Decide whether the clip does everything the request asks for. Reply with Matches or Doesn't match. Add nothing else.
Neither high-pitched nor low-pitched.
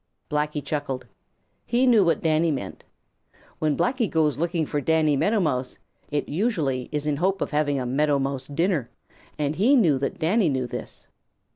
Matches